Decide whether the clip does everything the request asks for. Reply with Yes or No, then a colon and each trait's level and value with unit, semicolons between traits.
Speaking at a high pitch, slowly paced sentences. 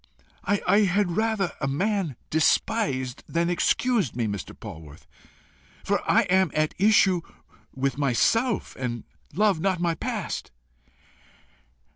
No: medium, 175 Hz; slow, 115 wpm